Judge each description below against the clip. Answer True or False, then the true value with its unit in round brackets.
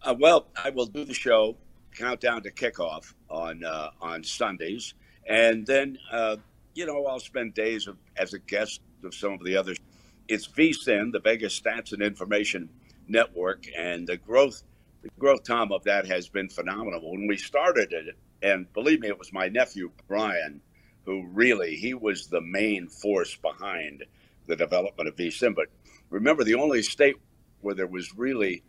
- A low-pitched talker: True (105 Hz)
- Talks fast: False (175 wpm)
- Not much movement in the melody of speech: False (3.8 semitones)